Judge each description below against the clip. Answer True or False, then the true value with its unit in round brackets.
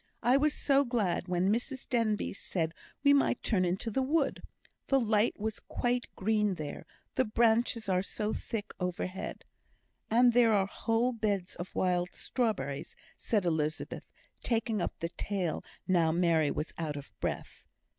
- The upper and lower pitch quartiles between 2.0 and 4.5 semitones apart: False (5.0 semitones)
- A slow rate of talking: False (155 wpm)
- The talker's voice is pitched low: False (210 Hz)